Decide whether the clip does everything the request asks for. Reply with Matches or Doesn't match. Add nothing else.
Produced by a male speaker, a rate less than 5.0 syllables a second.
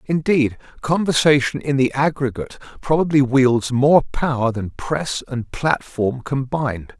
Matches